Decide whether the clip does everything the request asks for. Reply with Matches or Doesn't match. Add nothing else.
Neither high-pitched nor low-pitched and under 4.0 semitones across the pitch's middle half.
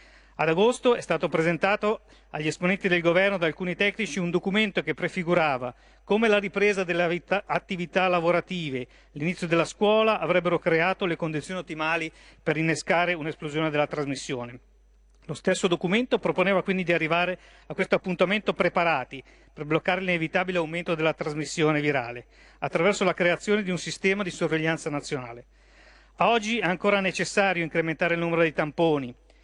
Matches